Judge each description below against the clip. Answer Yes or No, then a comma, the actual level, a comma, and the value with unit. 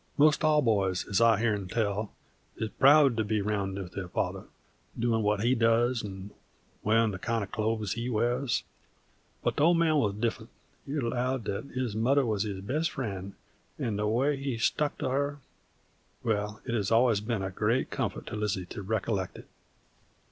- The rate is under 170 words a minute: No, average, 185 wpm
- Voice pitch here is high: No, low, 110 Hz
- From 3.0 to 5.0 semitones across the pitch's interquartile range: Yes, average, 3.7 semitones